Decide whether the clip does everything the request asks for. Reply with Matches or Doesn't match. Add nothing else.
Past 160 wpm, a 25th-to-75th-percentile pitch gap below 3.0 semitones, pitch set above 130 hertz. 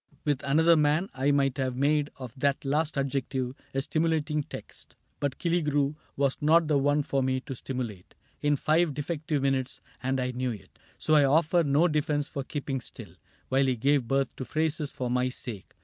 Matches